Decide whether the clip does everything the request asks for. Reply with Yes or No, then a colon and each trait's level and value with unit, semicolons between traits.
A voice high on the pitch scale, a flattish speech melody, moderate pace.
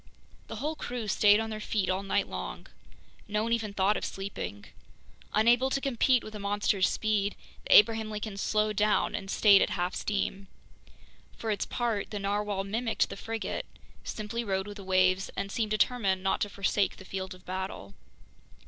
Yes: high, 205 Hz; narrow, 2.2 semitones; average, 180 wpm